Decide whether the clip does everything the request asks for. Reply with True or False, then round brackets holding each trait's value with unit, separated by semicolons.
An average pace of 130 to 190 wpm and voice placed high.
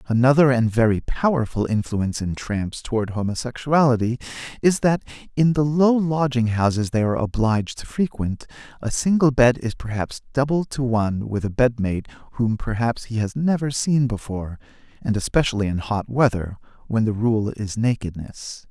False (155 wpm; 120 Hz)